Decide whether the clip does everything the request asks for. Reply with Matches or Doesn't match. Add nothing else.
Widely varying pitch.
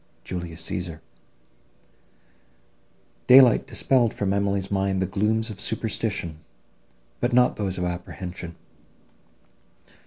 Doesn't match